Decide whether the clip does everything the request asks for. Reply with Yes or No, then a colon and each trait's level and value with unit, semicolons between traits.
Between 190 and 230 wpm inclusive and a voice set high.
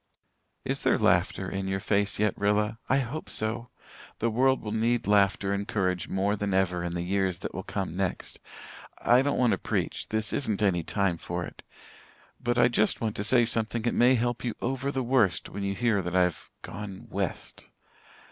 No: average, 195 wpm; low, 105 Hz